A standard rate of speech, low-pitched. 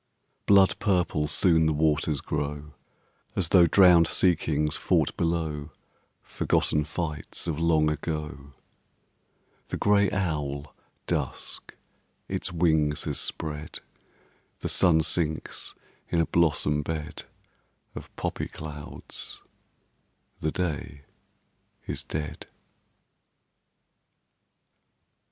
No: slow, 95 wpm; very low, 80 Hz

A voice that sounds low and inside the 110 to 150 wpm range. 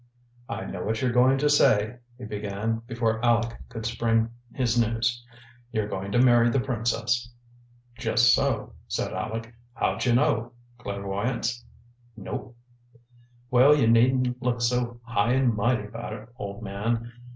Yes: low, 115 Hz; average, 145 wpm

